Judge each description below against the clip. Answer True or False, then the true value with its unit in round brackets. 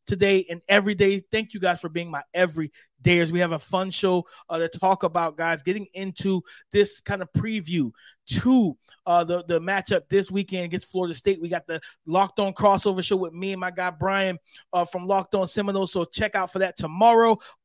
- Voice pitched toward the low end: False (185 Hz)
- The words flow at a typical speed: False (210 wpm)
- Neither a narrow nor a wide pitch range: False (2.3 semitones)